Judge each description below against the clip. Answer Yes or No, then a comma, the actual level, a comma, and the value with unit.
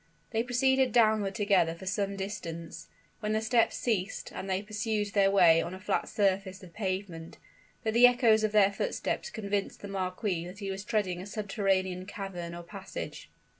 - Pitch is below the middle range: No, high, 200 Hz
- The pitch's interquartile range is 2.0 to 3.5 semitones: Yes, narrow, 2.4 semitones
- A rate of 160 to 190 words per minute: Yes, average, 175 wpm